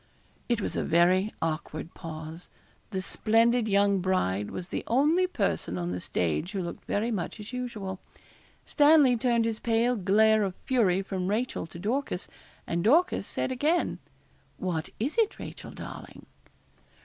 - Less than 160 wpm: Yes, average, 150 wpm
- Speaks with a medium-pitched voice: No, high, 205 Hz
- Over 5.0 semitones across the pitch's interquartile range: Yes, wide, 5.5 semitones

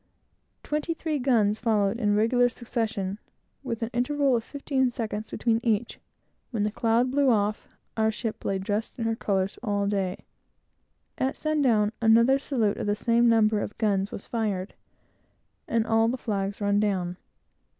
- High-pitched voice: Yes, high, 225 Hz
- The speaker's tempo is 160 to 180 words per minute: Yes, average, 165 wpm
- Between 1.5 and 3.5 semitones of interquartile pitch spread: Yes, average, 3.0 semitones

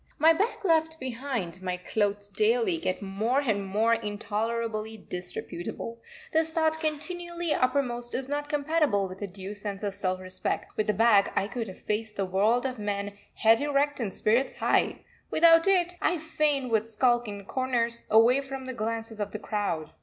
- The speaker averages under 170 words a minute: No, average, 175 wpm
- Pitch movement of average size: No, wide, 6.0 semitones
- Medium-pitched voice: No, high, 230 Hz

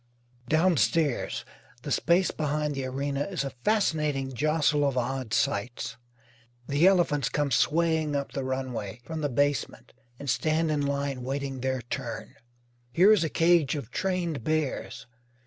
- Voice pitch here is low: No, medium, 145 Hz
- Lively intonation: No, average, 3.2 semitones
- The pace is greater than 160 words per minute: No, average, 145 wpm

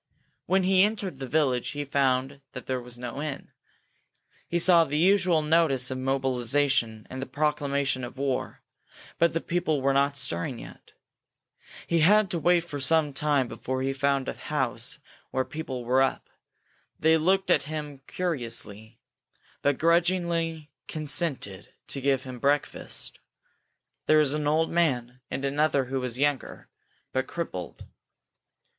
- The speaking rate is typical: Yes, average, 150 wpm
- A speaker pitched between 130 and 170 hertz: Yes, medium, 140 Hz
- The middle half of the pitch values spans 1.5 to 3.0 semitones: No, average, 3.7 semitones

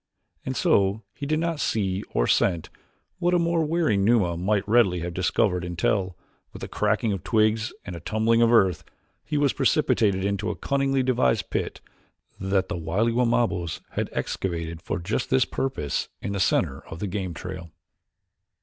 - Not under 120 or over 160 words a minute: No, average, 170 wpm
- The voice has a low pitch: Yes, low, 105 Hz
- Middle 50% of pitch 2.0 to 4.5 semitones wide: No, average, 4.9 semitones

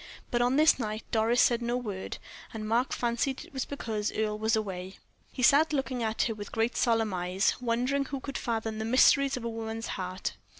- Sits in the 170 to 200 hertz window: No, high, 230 Hz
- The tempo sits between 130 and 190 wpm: No, fast, 205 wpm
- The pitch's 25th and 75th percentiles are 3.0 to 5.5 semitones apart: No, narrow, 2.6 semitones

